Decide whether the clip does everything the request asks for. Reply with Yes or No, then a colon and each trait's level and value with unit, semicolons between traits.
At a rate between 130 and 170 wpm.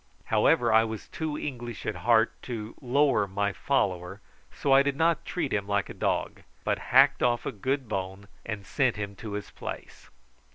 No: average, 180 wpm